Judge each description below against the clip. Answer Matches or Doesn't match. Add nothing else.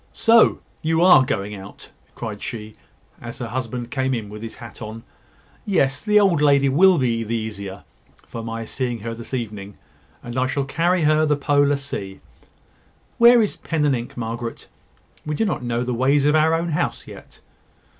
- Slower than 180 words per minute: Doesn't match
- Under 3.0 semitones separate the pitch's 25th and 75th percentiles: Doesn't match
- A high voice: Doesn't match